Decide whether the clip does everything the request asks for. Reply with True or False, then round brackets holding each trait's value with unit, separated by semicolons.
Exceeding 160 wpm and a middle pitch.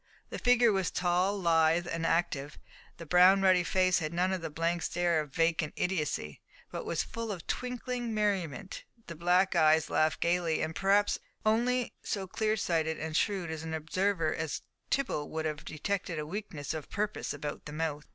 True (170 wpm; 175 Hz)